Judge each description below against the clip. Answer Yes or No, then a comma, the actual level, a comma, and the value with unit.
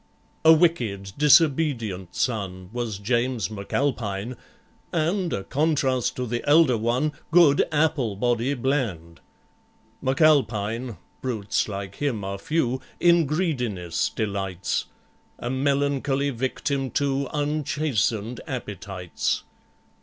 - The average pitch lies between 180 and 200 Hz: No, low, 125 Hz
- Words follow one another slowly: Yes, slow, 95 wpm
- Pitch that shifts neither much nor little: No, wide, 5.9 semitones